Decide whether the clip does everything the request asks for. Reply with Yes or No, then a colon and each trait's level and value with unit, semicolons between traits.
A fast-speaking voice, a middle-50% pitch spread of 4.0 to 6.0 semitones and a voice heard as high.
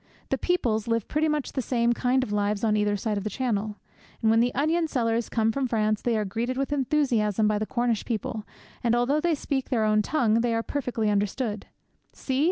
No: fast, 215 wpm; average, 3.4 semitones; high, 230 Hz